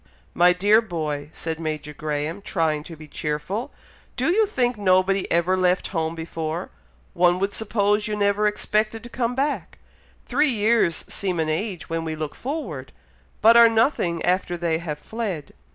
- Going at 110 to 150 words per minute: No, average, 165 wpm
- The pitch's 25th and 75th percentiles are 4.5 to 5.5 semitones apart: Yes, average, 5.2 semitones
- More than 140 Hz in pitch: Yes, medium, 185 Hz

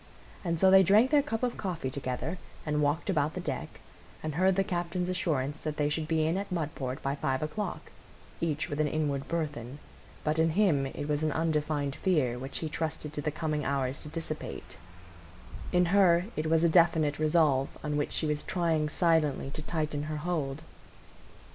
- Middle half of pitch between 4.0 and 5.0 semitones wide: No, average, 2.7 semitones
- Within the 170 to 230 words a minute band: Yes, average, 190 wpm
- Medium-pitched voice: Yes, medium, 155 Hz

